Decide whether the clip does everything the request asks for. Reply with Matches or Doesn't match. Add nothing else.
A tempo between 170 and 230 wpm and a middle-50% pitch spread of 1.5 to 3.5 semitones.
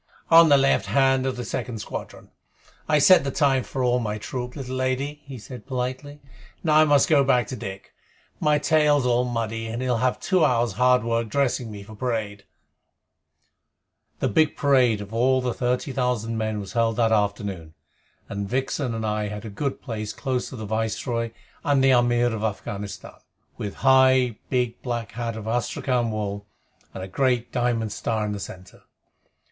Matches